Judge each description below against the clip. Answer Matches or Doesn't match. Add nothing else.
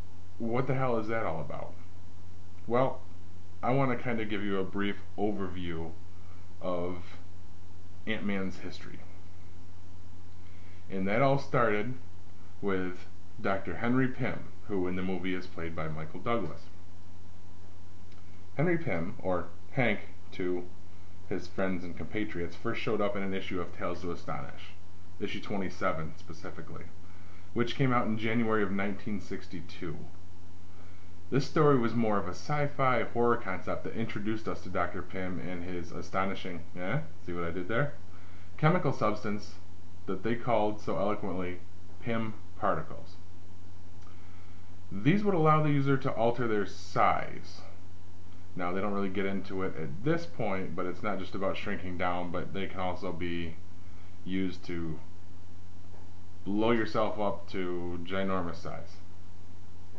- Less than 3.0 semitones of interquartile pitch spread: Matches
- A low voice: Matches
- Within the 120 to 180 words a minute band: Matches